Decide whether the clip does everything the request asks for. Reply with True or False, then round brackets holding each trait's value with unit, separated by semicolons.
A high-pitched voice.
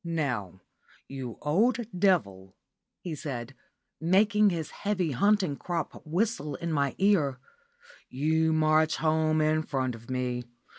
False (155 Hz)